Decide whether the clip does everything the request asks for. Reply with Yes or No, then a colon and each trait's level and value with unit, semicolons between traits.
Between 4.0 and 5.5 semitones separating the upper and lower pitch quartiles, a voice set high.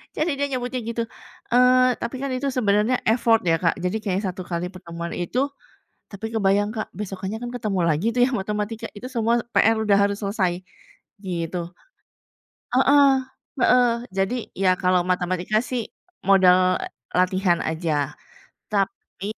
Yes: average, 4.3 semitones; high, 205 Hz